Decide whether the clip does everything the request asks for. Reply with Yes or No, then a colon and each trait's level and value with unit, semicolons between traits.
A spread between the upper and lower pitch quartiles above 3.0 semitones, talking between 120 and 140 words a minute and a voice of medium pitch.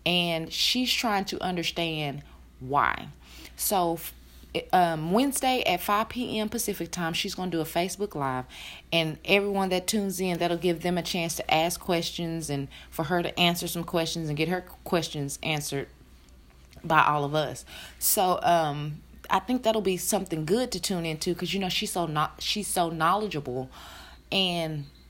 No: average, 3.8 semitones; average, 165 wpm; medium, 170 Hz